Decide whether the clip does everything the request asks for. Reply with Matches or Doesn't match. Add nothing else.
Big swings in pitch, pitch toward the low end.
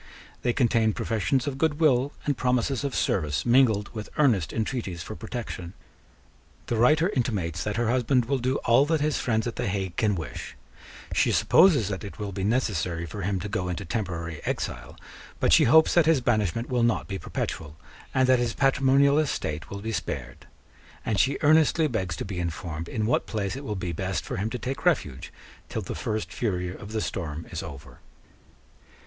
Matches